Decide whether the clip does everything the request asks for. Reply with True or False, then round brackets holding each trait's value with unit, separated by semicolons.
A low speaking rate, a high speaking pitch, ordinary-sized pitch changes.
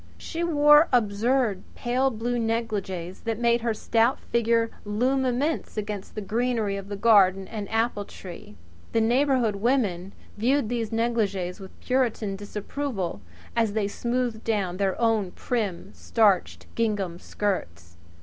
True (130 wpm; 225 Hz; 3.4 semitones)